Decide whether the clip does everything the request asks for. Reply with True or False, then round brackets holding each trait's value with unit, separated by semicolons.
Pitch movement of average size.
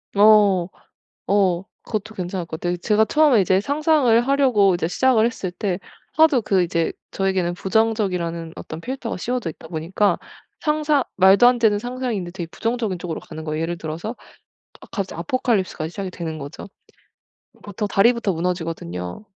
True (5.0 semitones)